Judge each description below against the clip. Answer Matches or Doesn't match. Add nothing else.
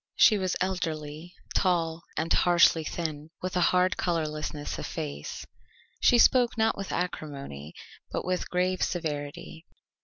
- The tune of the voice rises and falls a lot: Doesn't match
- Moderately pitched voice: Matches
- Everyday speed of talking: Doesn't match